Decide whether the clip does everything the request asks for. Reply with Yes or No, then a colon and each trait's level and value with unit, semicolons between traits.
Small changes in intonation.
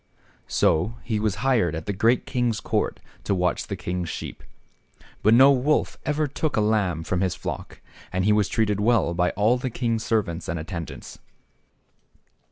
No: average, 4.9 semitones